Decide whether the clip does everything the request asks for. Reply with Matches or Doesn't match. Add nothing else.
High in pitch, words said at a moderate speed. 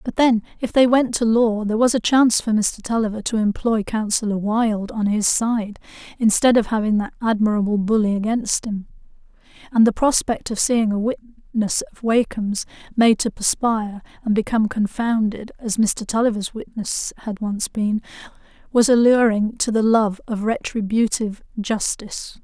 Matches